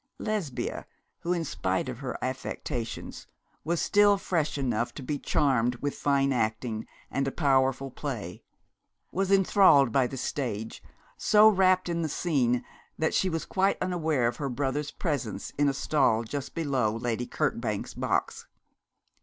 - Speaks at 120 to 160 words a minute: Yes, average, 150 wpm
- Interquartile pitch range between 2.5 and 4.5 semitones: No, average, 5.1 semitones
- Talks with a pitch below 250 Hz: Yes, medium, 140 Hz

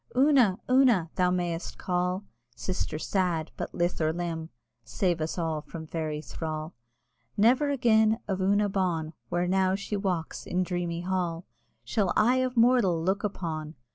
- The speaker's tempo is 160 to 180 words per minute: No, average, 150 wpm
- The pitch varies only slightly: No, average, 3.8 semitones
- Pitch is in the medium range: Yes, medium, 180 Hz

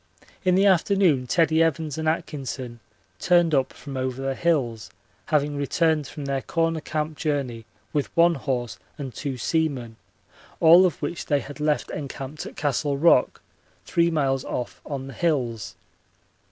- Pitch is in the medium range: Yes, medium, 145 Hz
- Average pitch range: Yes, average, 3.5 semitones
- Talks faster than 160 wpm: No, average, 155 wpm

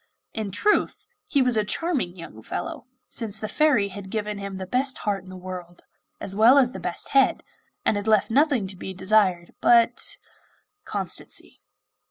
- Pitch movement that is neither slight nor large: Yes, average, 4.8 semitones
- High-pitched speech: Yes, high, 210 Hz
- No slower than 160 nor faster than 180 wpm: Yes, average, 175 wpm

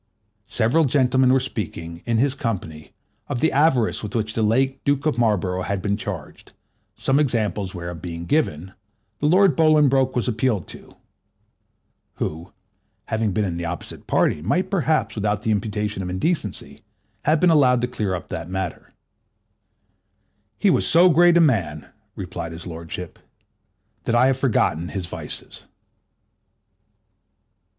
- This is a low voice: Yes, low, 110 Hz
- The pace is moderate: Yes, average, 145 wpm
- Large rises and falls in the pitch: Yes, wide, 6.8 semitones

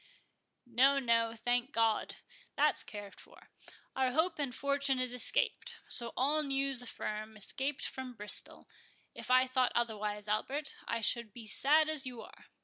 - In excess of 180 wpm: No, average, 145 wpm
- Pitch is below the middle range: No, very high, 250 Hz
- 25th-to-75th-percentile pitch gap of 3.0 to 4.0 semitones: Yes, average, 3.3 semitones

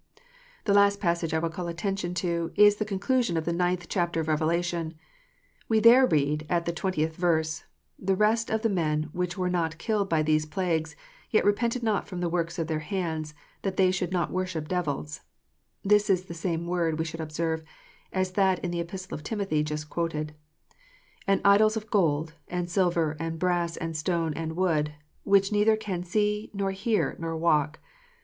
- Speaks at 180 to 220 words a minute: Yes, average, 190 wpm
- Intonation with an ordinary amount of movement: Yes, average, 3.3 semitones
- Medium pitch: Yes, medium, 175 Hz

